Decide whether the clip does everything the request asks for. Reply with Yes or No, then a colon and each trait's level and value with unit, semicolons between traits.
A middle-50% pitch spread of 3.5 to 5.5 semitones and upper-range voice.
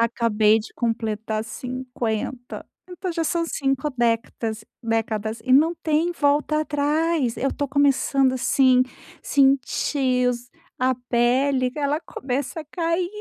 Yes: average, 3.8 semitones; very high, 260 Hz